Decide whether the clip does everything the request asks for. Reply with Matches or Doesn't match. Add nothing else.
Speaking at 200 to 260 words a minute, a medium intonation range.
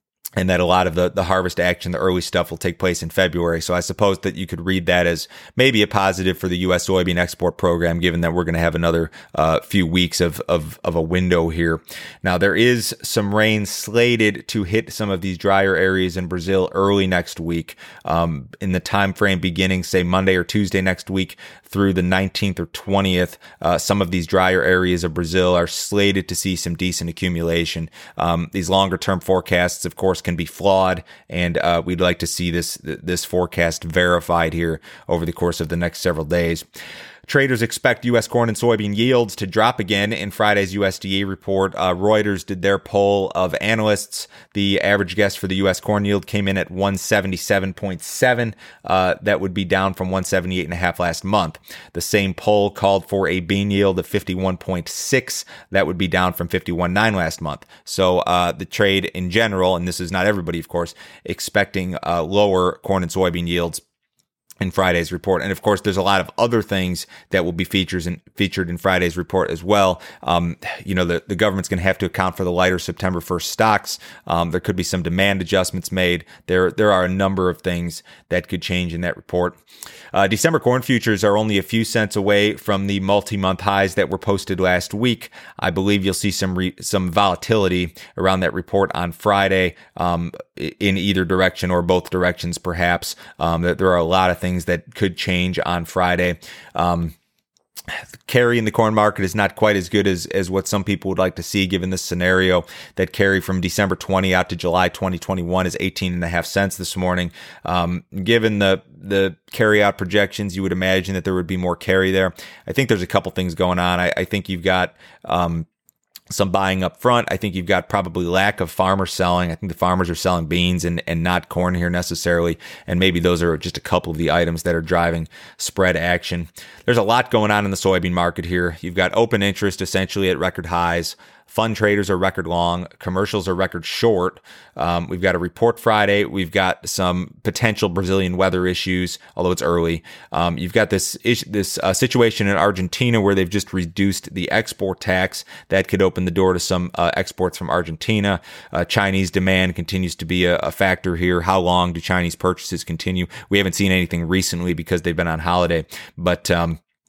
Doesn't match